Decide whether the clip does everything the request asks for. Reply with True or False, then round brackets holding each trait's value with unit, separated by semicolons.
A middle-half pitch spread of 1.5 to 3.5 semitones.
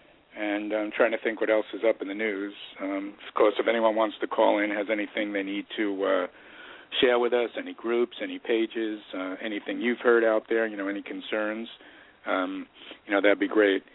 True (2.7 semitones)